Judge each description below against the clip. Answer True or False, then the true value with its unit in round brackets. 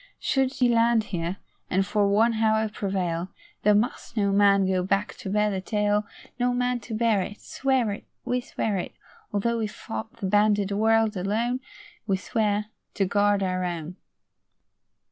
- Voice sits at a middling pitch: False (210 Hz)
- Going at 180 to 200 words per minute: False (165 wpm)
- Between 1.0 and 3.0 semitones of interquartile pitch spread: True (2.5 semitones)